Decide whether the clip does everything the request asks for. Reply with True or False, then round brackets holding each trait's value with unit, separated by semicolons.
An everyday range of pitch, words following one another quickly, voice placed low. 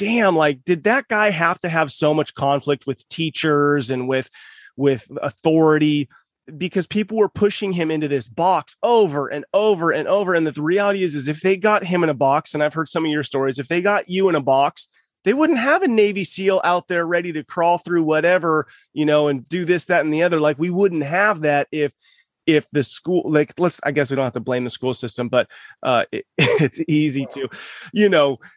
False (4.0 semitones; 225 wpm; 160 Hz)